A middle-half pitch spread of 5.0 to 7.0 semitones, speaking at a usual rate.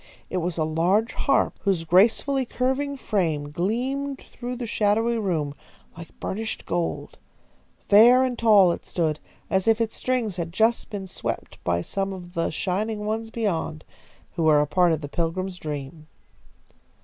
Yes: wide, 5.4 semitones; average, 160 wpm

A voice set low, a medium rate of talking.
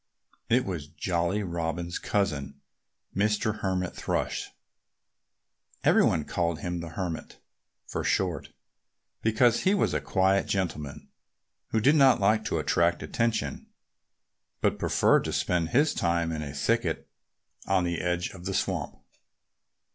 No: very low, 90 Hz; slow, 130 wpm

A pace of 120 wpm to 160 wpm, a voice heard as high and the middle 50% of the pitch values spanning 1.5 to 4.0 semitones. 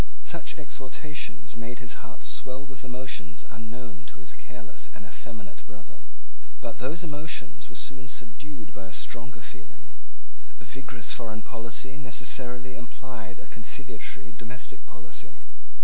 No: slow, 135 wpm; low, 120 Hz; average, 3.6 semitones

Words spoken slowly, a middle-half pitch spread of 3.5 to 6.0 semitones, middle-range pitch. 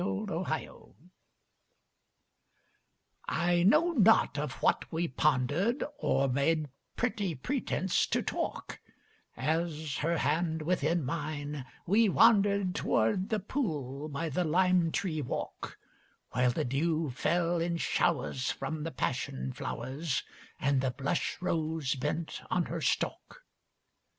Yes: slow, 120 wpm; average, 4.1 semitones; medium, 160 Hz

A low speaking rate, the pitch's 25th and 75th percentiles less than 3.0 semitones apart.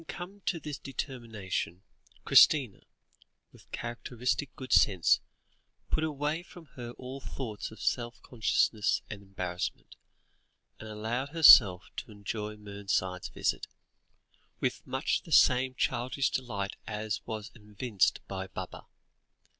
No: slow, 120 wpm; average, 4.4 semitones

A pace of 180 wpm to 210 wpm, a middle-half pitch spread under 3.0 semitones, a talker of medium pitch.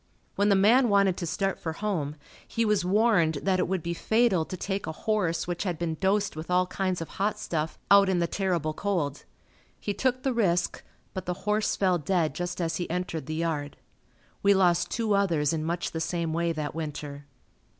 No: fast, 205 wpm; average, 3.5 semitones; medium, 180 Hz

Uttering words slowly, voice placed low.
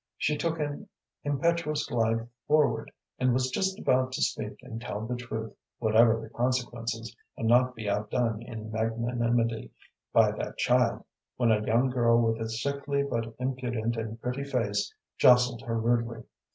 No: average, 155 wpm; low, 120 Hz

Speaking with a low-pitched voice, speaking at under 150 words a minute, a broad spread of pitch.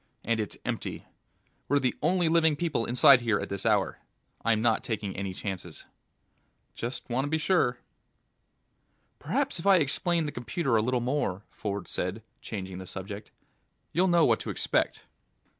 No: low, 120 Hz; average, 160 wpm; wide, 6.8 semitones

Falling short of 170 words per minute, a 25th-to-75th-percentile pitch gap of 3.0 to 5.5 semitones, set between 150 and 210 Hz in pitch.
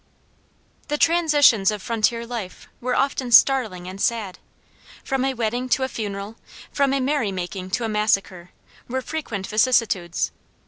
No: average, 140 wpm; average, 4.8 semitones; high, 230 Hz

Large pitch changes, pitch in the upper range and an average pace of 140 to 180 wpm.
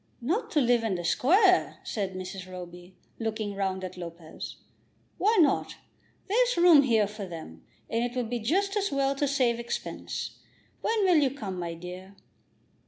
Yes: wide, 8.1 semitones; high, 230 Hz; average, 170 wpm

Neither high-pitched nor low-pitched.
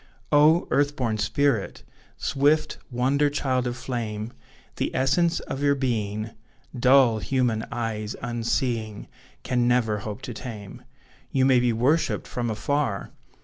No: low, 125 Hz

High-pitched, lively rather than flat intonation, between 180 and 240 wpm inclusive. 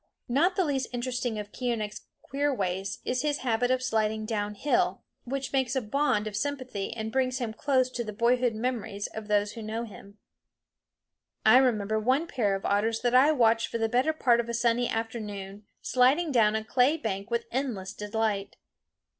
No: high, 235 Hz; average, 3.3 semitones; average, 185 wpm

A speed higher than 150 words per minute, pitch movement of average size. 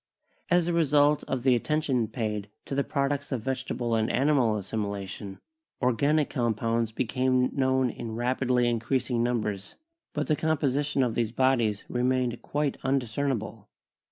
No: average, 140 wpm; average, 3.4 semitones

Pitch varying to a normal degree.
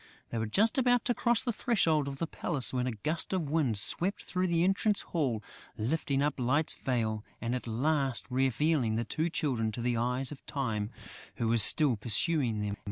No: wide, 5.9 semitones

